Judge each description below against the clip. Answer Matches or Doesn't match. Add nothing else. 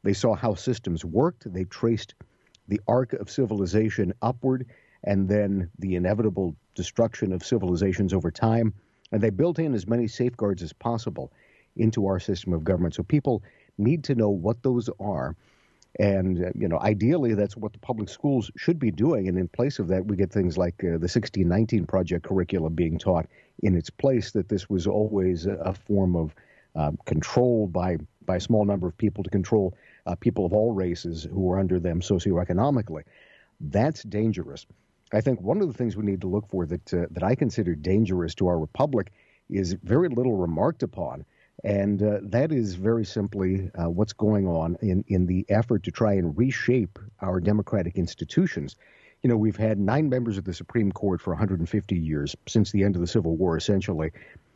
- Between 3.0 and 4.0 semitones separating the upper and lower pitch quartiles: Matches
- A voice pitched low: Matches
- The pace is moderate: Matches